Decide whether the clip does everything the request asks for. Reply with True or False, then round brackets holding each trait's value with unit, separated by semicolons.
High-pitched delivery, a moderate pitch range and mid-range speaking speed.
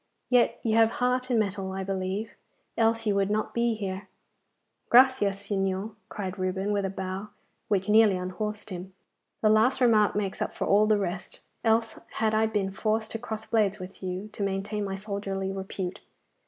False (205 Hz; 2.3 semitones; 180 wpm)